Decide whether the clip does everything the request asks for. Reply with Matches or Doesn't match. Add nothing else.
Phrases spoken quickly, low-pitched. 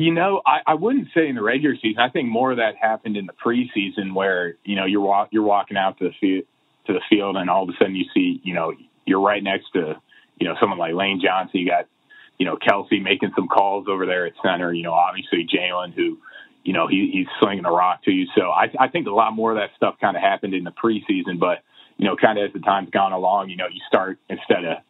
Matches